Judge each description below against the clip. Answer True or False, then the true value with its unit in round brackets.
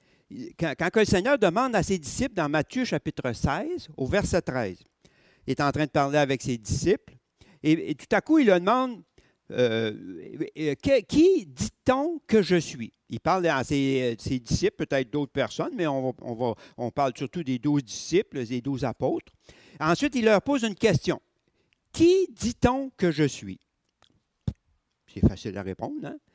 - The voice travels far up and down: True (8.7 semitones)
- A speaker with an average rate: True (175 wpm)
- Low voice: False (155 Hz)